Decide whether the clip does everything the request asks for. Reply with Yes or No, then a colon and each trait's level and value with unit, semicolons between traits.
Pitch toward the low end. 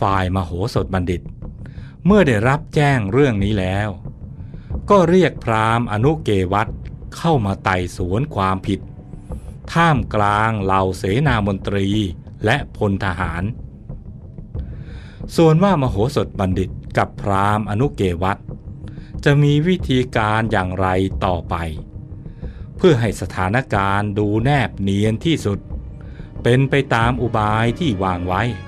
Yes: low, 105 Hz